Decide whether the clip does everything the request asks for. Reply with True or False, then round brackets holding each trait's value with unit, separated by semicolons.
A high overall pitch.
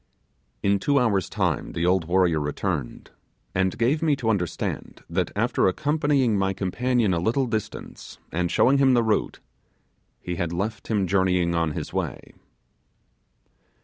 False (100 Hz)